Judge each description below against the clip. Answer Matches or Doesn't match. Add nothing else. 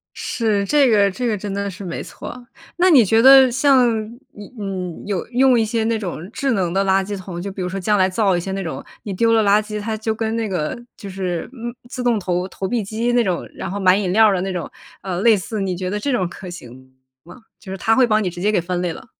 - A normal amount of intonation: Matches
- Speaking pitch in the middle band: Doesn't match